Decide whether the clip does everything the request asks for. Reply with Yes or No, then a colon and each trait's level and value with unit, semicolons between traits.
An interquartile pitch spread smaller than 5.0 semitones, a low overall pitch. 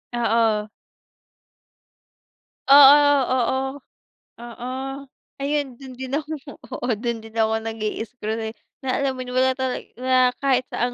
No: narrow, 2.6 semitones; very high, 250 Hz